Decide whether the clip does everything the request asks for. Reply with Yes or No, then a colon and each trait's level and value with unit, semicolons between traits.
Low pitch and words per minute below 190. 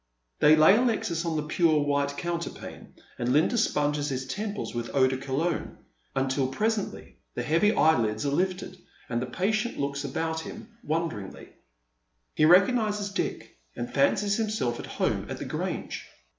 No: medium, 155 Hz; average, 155 wpm